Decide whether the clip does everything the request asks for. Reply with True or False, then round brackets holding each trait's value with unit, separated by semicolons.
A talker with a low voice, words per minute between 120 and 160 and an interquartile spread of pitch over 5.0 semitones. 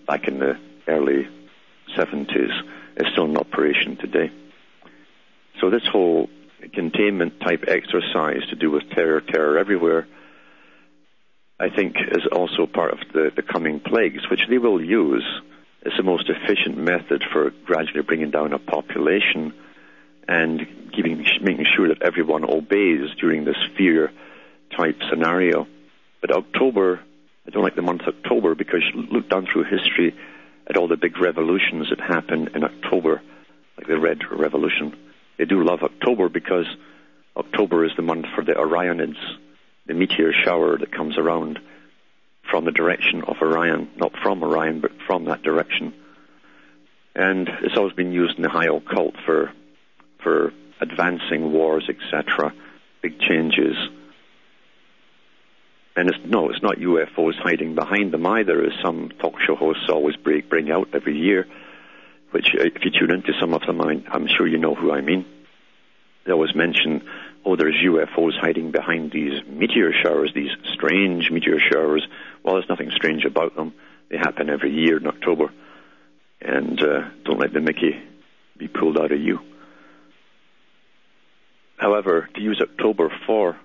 True (75 Hz; 150 wpm; 5.6 semitones)